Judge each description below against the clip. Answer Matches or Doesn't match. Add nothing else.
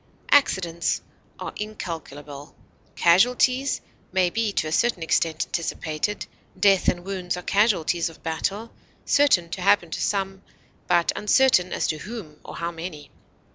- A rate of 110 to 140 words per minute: Matches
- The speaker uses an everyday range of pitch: Matches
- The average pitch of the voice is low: Doesn't match